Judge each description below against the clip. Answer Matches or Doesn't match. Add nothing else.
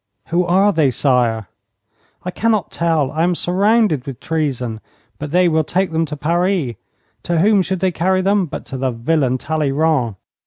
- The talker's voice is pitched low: Doesn't match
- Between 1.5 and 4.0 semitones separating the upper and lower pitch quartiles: Doesn't match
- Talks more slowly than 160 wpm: Doesn't match